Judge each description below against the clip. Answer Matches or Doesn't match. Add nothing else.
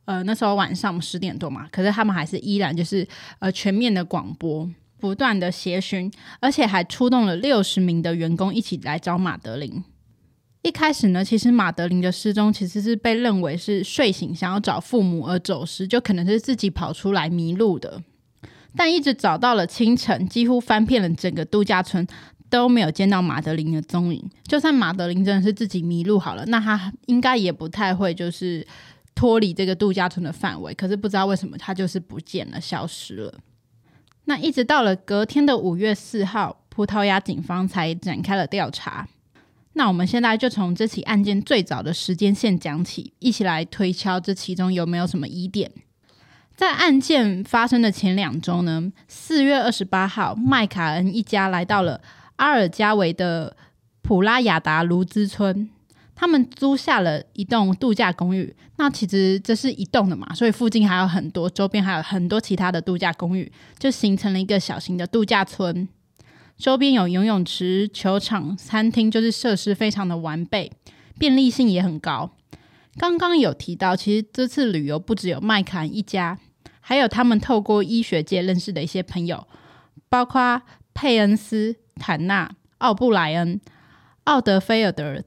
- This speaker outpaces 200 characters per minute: Matches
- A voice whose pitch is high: Matches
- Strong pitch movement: Doesn't match